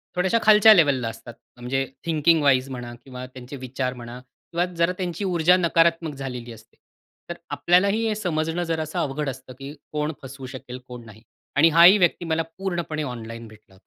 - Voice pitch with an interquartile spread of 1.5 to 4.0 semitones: No, average, 5.1 semitones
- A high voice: No, medium, 150 Hz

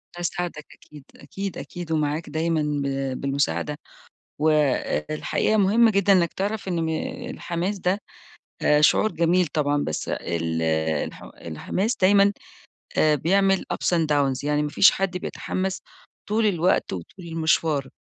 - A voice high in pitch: No, medium, 165 Hz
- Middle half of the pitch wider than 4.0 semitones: Yes, average, 4.7 semitones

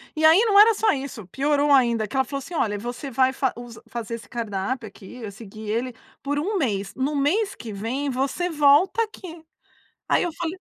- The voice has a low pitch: No, very high, 265 Hz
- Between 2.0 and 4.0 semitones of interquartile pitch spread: No, wide, 5.4 semitones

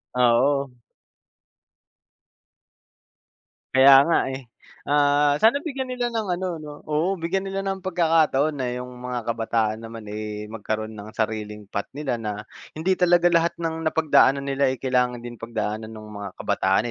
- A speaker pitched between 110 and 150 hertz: Yes, low, 135 Hz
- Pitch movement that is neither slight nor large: No, wide, 6.5 semitones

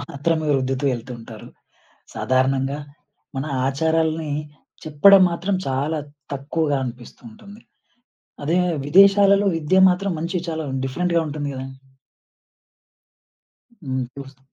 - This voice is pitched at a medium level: Yes, medium, 150 Hz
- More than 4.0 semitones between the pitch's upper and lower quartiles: Yes, average, 4.6 semitones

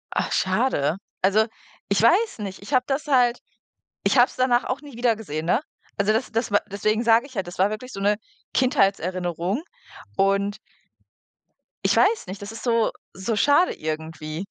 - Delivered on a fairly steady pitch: No, average, 4.8 semitones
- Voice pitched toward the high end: Yes, high, 215 Hz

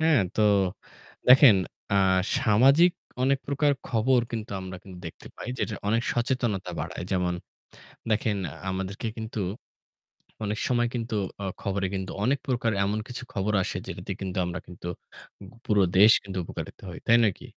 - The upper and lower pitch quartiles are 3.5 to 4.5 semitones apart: Yes, average, 4.2 semitones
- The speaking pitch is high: No, low, 110 Hz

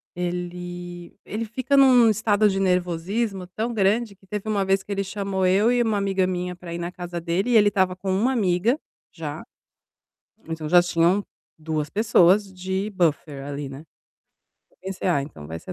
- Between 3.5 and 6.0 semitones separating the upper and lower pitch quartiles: No, average, 2.9 semitones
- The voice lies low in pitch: No, high, 190 Hz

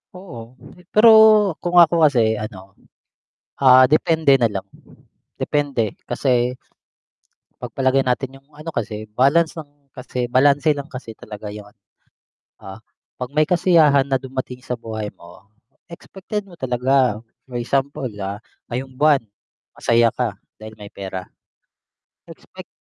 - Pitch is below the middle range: Yes, low, 130 Hz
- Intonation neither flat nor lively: Yes, average, 4.2 semitones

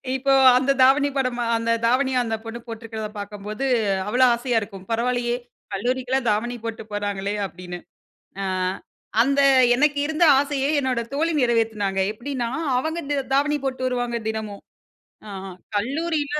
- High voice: Yes, high, 240 Hz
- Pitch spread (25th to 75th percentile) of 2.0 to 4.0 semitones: Yes, average, 3.7 semitones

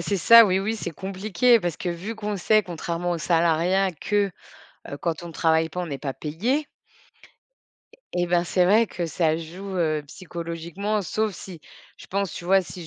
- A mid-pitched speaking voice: Yes, medium, 180 Hz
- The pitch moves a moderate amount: Yes, average, 3.1 semitones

